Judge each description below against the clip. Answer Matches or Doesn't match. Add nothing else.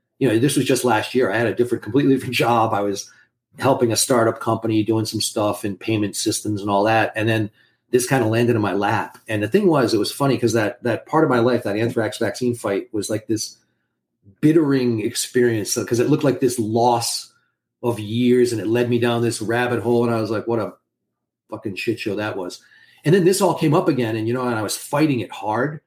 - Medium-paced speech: Doesn't match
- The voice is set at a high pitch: Doesn't match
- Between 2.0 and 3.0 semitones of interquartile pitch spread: Matches